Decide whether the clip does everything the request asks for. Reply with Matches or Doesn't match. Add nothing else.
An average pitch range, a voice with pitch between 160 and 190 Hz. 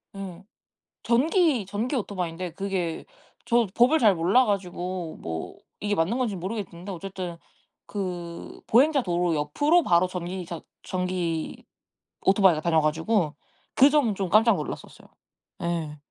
Matches